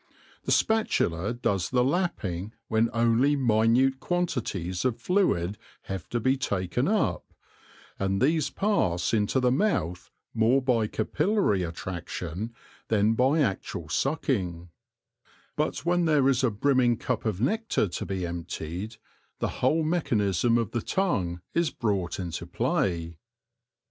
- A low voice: Yes, low, 115 Hz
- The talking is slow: Yes, slow, 130 wpm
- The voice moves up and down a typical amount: No, wide, 6.6 semitones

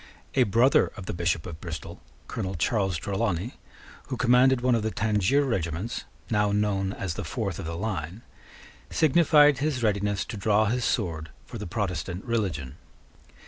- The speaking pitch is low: Yes, low, 105 Hz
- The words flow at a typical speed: Yes, average, 160 wpm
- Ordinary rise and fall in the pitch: Yes, average, 4.5 semitones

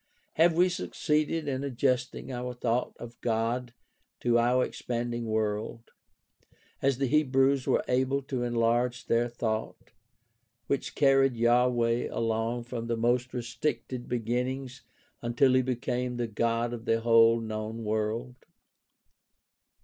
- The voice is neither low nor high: No, low, 120 Hz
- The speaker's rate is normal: No, slow, 125 wpm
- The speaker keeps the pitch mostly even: Yes, narrow, 1.9 semitones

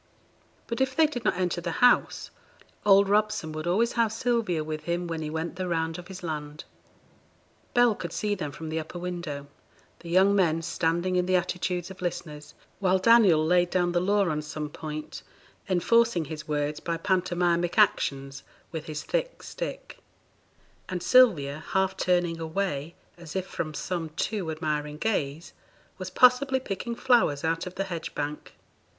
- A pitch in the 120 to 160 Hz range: No, medium, 175 Hz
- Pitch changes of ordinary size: Yes, average, 3.8 semitones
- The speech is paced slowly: No, average, 170 wpm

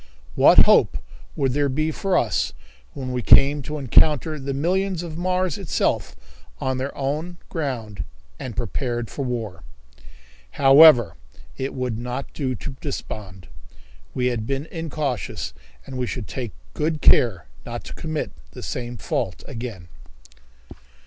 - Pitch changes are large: No, average, 4.2 semitones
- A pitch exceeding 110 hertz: Yes, low, 135 Hz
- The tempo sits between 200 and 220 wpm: No, average, 140 wpm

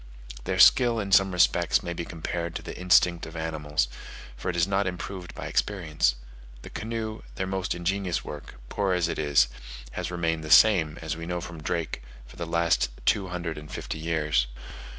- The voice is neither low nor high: No, very low, 85 Hz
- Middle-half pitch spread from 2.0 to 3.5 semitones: Yes, average, 3.0 semitones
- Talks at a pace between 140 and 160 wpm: No, average, 190 wpm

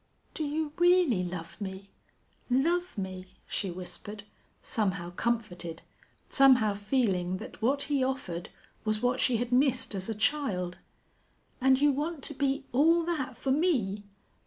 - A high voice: Yes, high, 245 Hz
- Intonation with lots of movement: Yes, wide, 6.7 semitones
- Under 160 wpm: Yes, average, 140 wpm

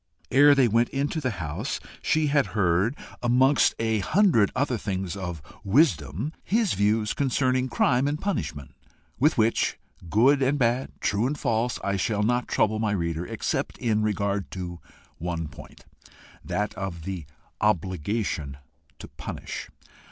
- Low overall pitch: Yes, low, 110 Hz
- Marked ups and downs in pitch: Yes, wide, 5.7 semitones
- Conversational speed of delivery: Yes, average, 145 wpm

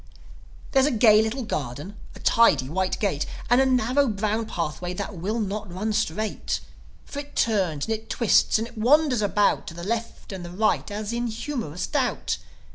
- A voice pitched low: No, high, 215 Hz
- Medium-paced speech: Yes, average, 185 wpm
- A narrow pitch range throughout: No, average, 3.8 semitones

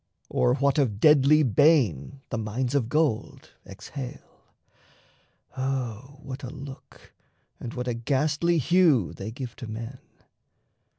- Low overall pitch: Yes, low, 130 Hz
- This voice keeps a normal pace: No, slow, 125 wpm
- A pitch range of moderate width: Yes, average, 3.5 semitones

